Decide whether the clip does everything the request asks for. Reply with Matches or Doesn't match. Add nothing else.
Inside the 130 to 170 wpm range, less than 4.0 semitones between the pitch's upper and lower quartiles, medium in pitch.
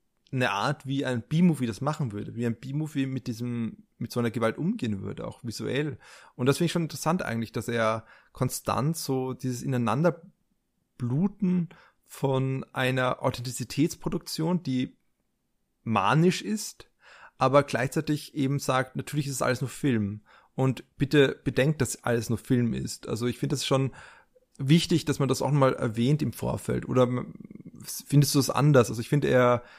Doesn't match